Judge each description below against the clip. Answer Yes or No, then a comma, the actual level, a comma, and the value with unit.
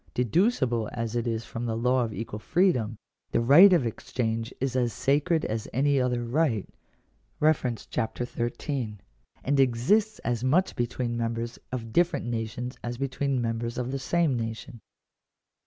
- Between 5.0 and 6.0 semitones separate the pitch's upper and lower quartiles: No, average, 3.1 semitones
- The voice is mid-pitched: No, low, 120 Hz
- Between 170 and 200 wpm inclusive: No, average, 150 wpm